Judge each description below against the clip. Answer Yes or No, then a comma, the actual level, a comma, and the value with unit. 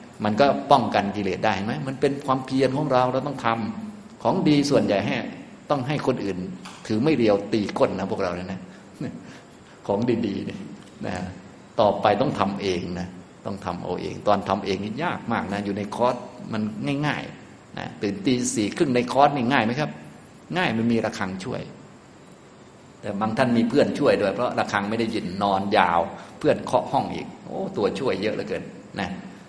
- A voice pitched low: Yes, low, 115 Hz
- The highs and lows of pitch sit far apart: Yes, wide, 5.8 semitones